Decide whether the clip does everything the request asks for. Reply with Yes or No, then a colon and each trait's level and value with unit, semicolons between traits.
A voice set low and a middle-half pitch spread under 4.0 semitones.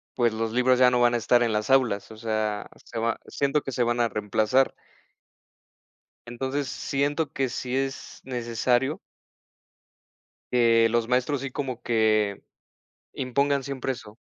Yes: low, 120 Hz; average, 2.8 semitones